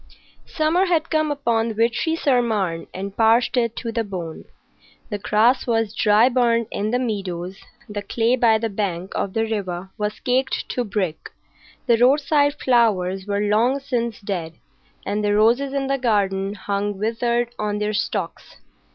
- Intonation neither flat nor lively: Yes, average, 3.3 semitones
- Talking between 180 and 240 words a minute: No, average, 160 wpm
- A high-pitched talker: Yes, high, 225 Hz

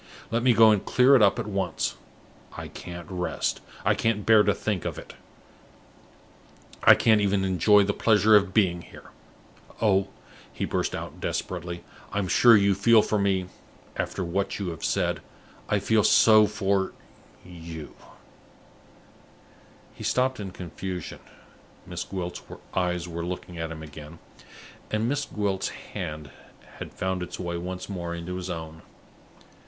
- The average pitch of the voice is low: Yes, very low, 95 Hz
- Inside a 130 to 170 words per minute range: Yes, average, 150 wpm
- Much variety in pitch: No, average, 3.2 semitones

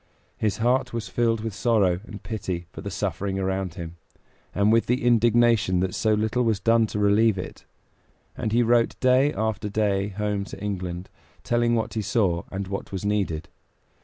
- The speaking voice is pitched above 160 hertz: No, low, 105 Hz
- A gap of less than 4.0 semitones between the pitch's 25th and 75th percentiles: Yes, average, 3.0 semitones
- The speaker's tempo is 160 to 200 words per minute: Yes, average, 175 wpm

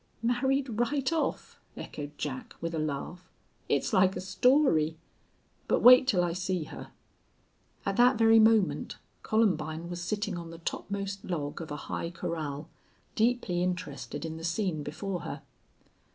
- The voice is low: No, medium, 180 Hz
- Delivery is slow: No, average, 150 wpm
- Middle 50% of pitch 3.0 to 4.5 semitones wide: No, wide, 5.6 semitones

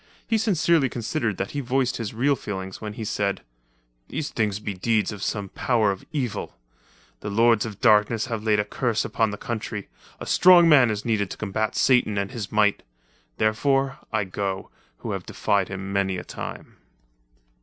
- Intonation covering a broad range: No, average, 3.4 semitones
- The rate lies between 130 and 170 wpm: No, average, 180 wpm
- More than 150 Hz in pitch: No, low, 110 Hz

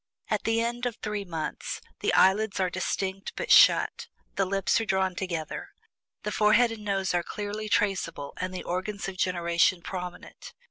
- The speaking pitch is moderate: No, high, 195 Hz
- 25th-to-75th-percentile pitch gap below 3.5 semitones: Yes, narrow, 2.6 semitones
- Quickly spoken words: No, average, 170 wpm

